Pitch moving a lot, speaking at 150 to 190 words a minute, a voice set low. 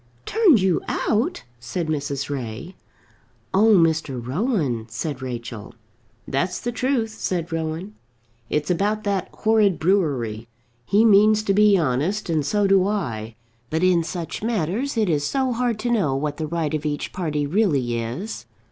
No: wide, 6.7 semitones; average, 155 wpm; medium, 170 Hz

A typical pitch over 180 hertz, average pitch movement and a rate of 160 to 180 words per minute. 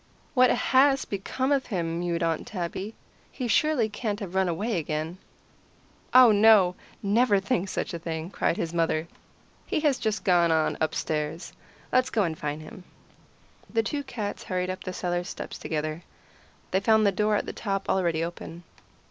Yes: high, 190 Hz; average, 4.8 semitones; average, 170 wpm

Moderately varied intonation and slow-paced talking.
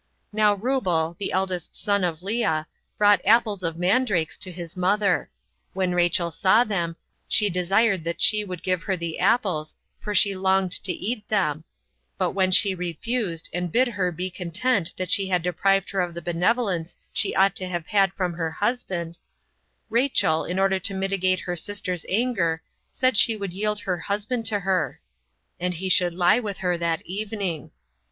No: average, 3.0 semitones; average, 175 wpm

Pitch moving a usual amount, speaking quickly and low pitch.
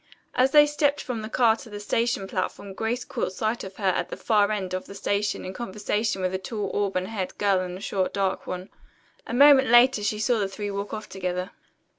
No: average, 3.2 semitones; fast, 225 wpm; high, 205 Hz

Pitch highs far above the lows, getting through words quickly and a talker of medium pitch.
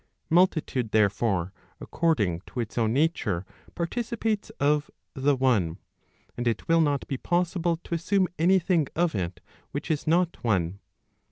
No: wide, 7.6 semitones; average, 150 wpm; medium, 145 Hz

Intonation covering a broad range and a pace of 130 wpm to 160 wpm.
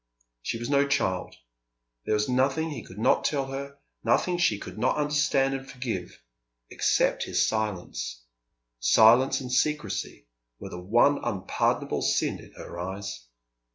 Yes: wide, 6.6 semitones; average, 145 wpm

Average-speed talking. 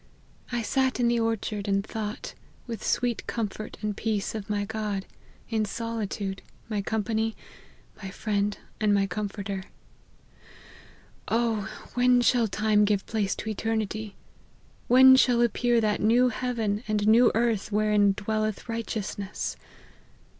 No: slow, 125 wpm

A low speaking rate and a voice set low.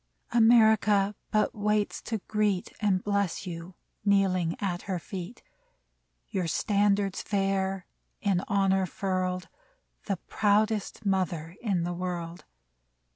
No: slow, 110 wpm; high, 195 Hz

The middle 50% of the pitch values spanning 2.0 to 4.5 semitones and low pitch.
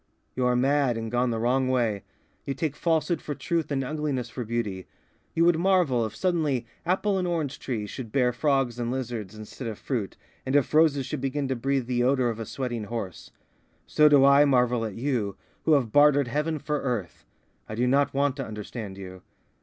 Yes: average, 3.8 semitones; low, 130 Hz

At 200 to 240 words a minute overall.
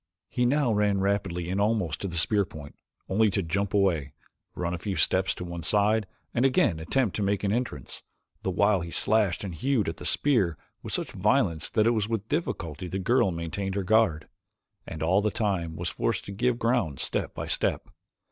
Yes: fast, 205 wpm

